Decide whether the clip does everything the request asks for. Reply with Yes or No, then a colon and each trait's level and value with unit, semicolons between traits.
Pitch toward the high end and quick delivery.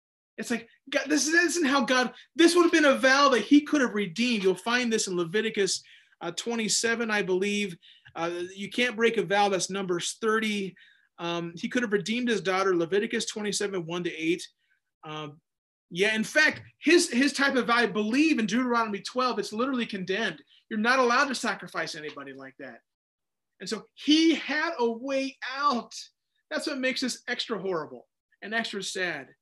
No: high, 230 Hz; average, 180 wpm